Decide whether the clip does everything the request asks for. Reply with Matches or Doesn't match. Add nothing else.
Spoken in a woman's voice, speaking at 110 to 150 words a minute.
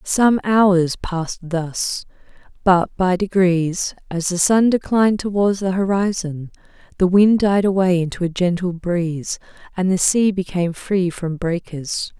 Matches